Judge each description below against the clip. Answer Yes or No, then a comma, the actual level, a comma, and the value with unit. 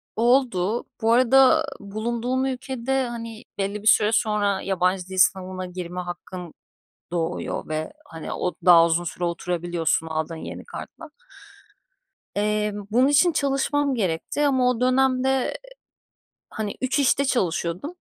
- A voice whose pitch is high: Yes, high, 210 Hz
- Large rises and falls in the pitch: Yes, wide, 6.3 semitones